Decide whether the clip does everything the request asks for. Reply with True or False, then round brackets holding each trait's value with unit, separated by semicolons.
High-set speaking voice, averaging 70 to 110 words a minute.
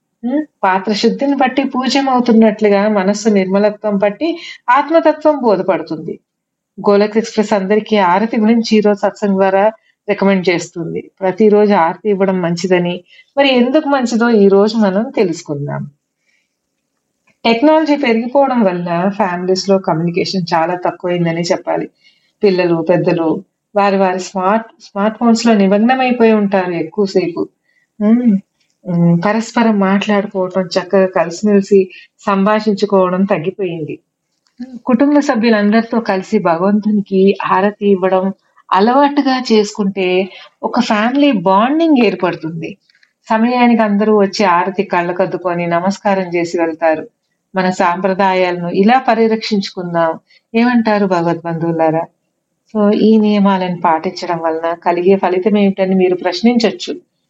True (200 Hz; 100 wpm)